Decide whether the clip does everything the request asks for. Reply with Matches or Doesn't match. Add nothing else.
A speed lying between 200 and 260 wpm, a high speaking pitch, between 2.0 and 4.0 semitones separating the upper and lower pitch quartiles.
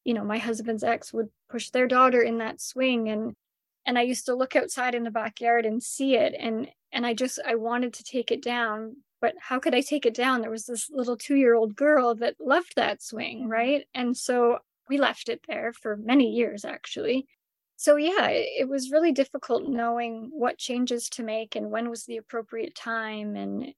Matches